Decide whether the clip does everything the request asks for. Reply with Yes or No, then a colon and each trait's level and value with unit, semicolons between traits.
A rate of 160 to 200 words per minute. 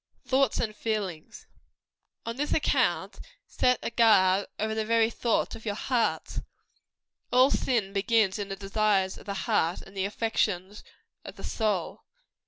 No: average, 150 wpm